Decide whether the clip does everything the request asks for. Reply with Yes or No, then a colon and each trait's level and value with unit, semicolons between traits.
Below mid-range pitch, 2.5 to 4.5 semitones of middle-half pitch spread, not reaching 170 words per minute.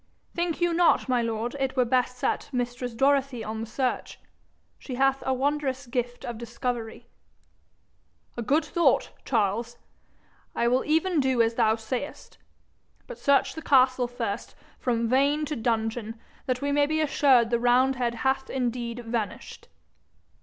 No: very high, 250 Hz; average, 2.8 semitones; average, 150 wpm